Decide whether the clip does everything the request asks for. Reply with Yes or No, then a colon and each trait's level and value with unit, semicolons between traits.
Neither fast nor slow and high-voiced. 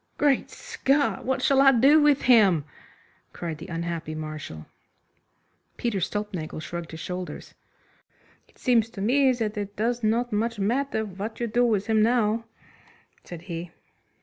Yes: average, 150 wpm; high, 215 Hz